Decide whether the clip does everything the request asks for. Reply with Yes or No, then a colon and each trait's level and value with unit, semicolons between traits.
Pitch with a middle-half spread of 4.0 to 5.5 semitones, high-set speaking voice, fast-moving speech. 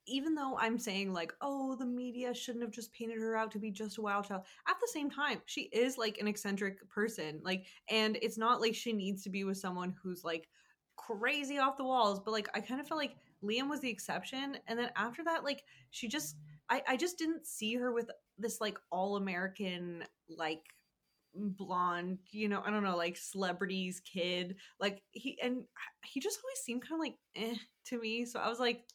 Yes: average, 4.4 semitones; high, 220 Hz; fast, 215 wpm